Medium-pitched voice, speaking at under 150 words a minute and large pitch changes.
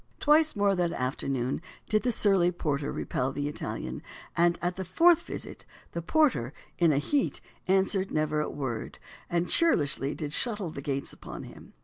No: medium, 170 Hz; average, 165 wpm; wide, 6.0 semitones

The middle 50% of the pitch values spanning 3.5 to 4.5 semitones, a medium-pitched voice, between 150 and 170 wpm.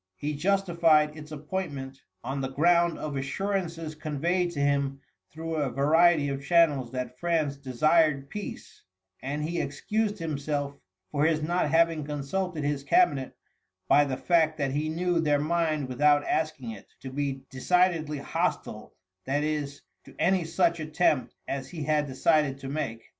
No: average, 3.1 semitones; medium, 150 Hz; average, 155 wpm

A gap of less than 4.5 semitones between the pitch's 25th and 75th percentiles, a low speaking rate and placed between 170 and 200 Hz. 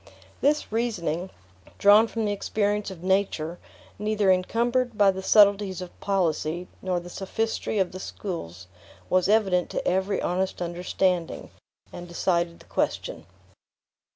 Yes: average, 2.9 semitones; slow, 130 wpm; high, 190 Hz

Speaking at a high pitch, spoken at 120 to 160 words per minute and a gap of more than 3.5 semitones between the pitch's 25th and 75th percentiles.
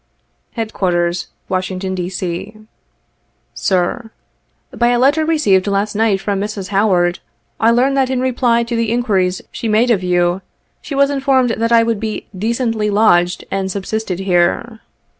Yes: high, 215 Hz; average, 155 wpm; average, 4.0 semitones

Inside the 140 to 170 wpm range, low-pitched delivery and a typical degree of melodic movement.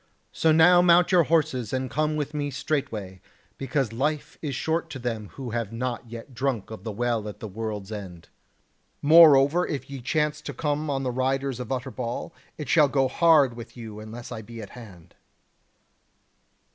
No: average, 180 wpm; low, 130 Hz; average, 4.7 semitones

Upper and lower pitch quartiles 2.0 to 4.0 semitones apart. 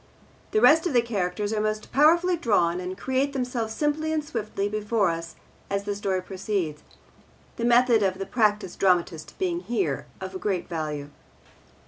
No: average, 5.2 semitones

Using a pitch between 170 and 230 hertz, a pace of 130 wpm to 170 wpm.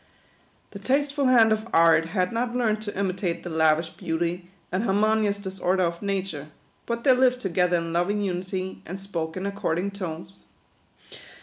Yes: high, 190 Hz; average, 165 wpm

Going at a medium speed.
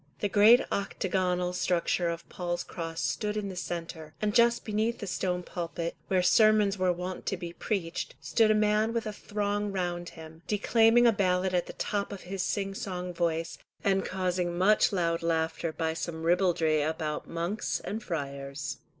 Yes: average, 175 wpm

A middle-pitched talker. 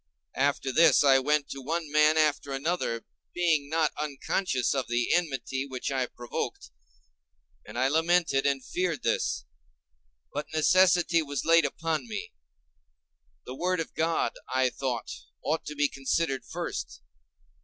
Yes: medium, 145 Hz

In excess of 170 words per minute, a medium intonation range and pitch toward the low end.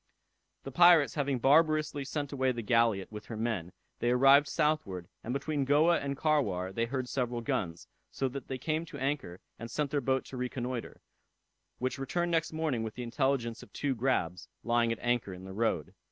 Yes: average, 190 wpm; average, 3.7 semitones; low, 130 Hz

